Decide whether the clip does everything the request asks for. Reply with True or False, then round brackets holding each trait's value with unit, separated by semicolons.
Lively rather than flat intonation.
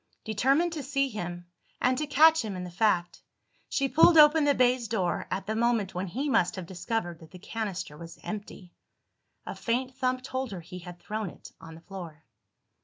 True (6.6 semitones)